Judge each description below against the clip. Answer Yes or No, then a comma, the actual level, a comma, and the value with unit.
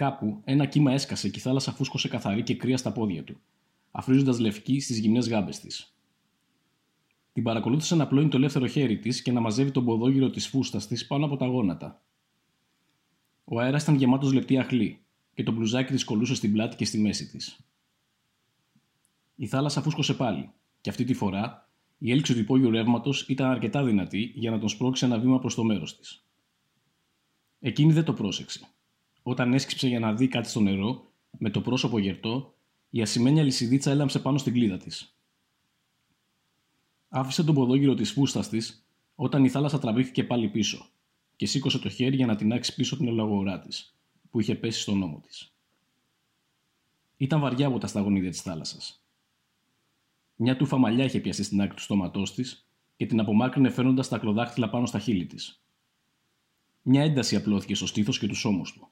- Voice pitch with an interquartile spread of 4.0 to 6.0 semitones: No, average, 3.4 semitones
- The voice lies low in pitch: Yes, low, 125 Hz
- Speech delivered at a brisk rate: Yes, fast, 175 wpm